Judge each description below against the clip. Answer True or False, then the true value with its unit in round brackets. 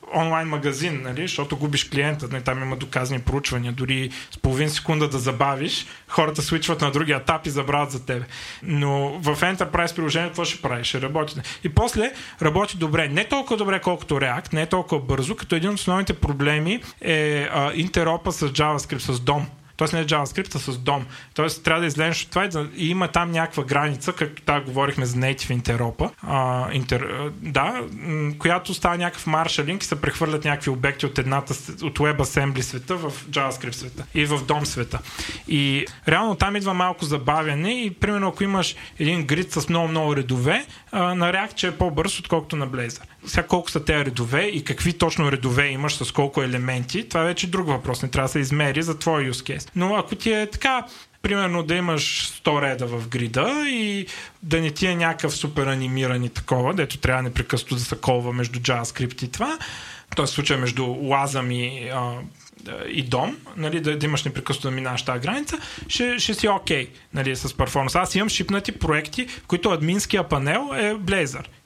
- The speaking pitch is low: False (150 Hz)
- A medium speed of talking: False (185 wpm)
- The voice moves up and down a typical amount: True (4.2 semitones)